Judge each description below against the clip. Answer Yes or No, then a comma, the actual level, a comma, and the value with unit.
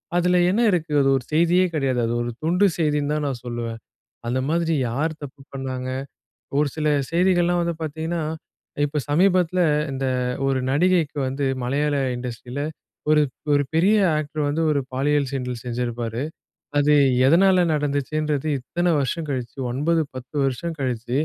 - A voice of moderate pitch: Yes, medium, 145 Hz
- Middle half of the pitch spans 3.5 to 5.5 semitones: Yes, average, 4.2 semitones